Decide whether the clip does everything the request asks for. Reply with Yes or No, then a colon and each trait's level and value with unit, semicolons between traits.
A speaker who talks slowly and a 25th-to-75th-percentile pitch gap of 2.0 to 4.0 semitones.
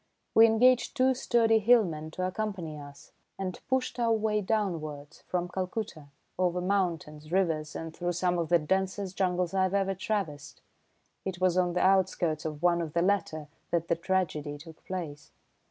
No: average, 165 wpm; average, 3.5 semitones